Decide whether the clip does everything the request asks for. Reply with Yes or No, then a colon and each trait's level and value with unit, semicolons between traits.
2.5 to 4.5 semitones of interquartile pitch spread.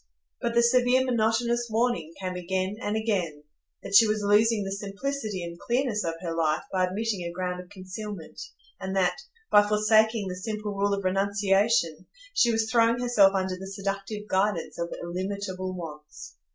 Yes: average, 3.1 semitones